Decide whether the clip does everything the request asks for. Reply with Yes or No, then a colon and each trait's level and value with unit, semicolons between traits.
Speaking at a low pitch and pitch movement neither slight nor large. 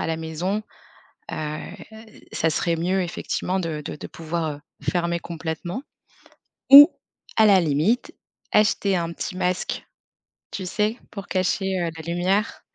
No: medium, 175 Hz; average, 3.2 semitones